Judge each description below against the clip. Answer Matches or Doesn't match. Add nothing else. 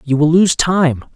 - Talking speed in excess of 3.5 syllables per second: Matches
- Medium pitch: Matches